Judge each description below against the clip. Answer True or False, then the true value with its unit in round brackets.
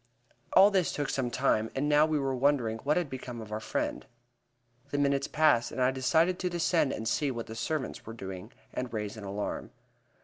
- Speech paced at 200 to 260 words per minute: True (205 wpm)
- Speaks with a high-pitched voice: False (130 Hz)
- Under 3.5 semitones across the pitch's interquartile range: False (4.8 semitones)